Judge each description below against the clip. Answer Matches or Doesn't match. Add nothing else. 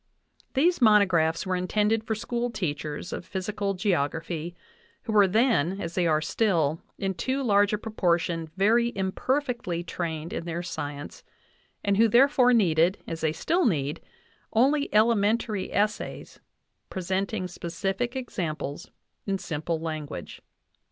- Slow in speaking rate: Matches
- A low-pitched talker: Doesn't match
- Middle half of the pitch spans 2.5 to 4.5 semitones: Doesn't match